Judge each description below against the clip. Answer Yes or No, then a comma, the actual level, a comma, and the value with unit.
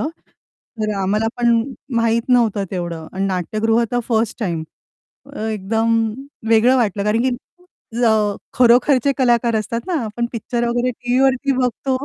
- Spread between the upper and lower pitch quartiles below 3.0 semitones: Yes, narrow, 2.4 semitones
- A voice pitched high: Yes, high, 230 Hz